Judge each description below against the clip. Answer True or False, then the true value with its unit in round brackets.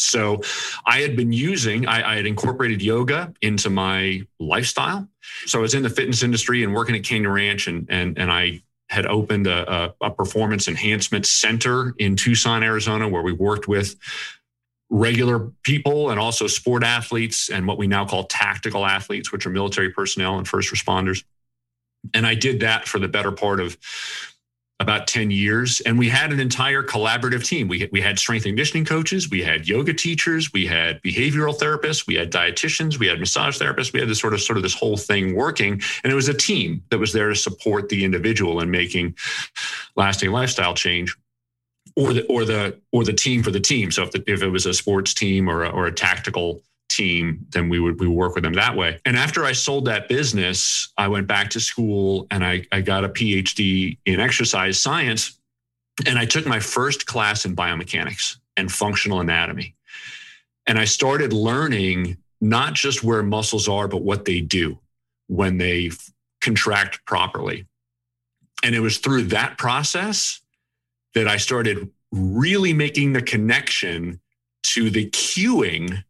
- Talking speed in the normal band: True (185 wpm)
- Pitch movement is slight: False (4.3 semitones)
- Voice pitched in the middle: False (105 Hz)